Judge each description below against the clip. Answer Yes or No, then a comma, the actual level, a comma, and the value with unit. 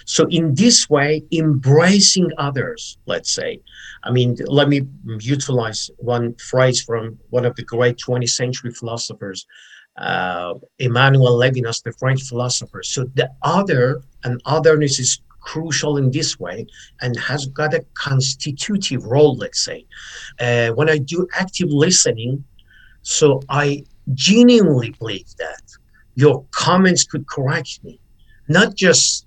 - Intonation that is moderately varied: Yes, average, 4.0 semitones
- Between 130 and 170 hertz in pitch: Yes, low, 135 Hz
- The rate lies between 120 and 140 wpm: Yes, slow, 135 wpm